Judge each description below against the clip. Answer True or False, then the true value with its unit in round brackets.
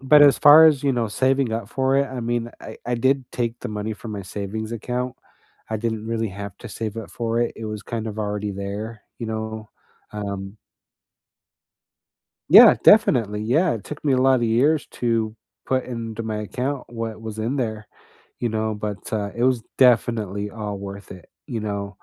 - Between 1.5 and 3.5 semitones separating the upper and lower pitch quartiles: True (2.8 semitones)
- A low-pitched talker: True (115 Hz)